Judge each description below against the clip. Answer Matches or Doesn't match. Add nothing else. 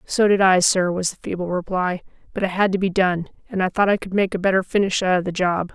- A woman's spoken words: Matches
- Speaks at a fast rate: Matches